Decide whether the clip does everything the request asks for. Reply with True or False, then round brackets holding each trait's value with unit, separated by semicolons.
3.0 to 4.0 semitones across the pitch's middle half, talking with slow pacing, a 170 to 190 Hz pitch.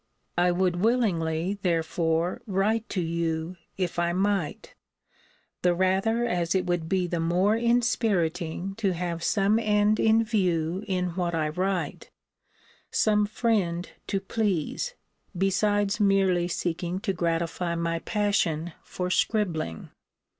True (3.3 semitones; 125 wpm; 185 Hz)